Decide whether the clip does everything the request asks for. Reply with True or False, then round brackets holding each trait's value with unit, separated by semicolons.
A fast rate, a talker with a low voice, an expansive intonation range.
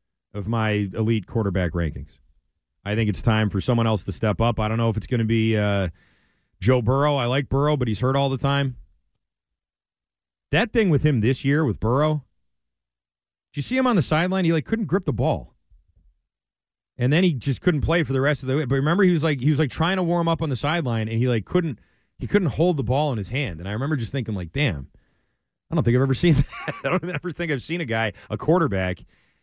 True (245 wpm; 130 Hz; 6.5 semitones)